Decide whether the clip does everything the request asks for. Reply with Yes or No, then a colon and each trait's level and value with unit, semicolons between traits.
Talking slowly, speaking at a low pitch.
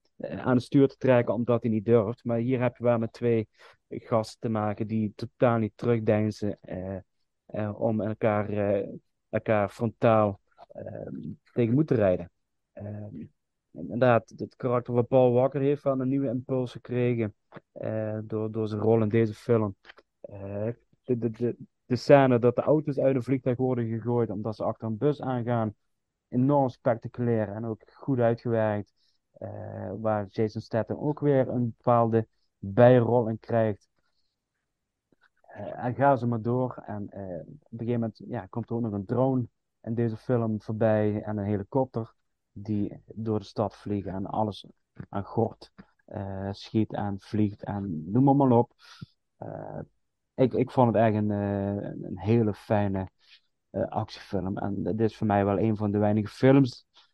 No: average, 170 wpm; low, 115 Hz